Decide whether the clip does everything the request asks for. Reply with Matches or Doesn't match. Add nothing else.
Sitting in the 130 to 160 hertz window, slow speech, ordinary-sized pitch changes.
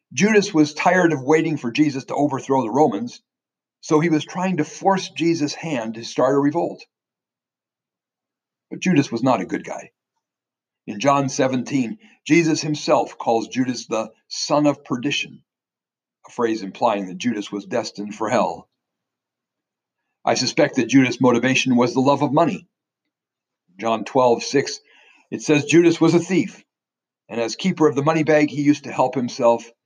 Doesn't match